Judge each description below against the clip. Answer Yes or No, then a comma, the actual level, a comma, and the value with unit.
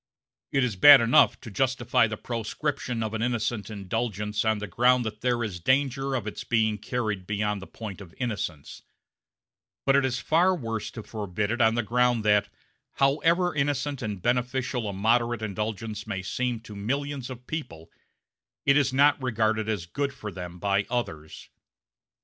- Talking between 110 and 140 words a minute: No, average, 170 wpm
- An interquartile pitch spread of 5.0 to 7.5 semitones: No, average, 3.5 semitones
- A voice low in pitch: Yes, low, 115 Hz